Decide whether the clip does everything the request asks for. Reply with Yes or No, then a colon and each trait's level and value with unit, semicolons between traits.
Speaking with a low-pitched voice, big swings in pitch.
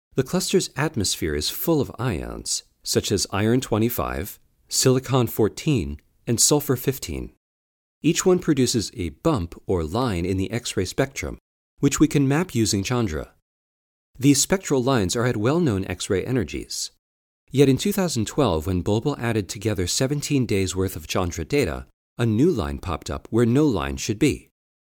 Yes: low, 110 Hz; wide, 7.7 semitones